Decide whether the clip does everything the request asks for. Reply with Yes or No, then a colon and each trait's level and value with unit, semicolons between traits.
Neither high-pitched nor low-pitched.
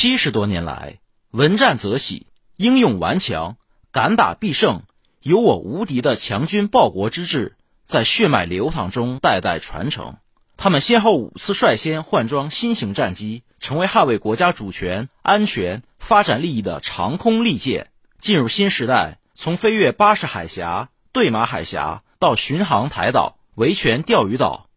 Yes: medium, 165 Hz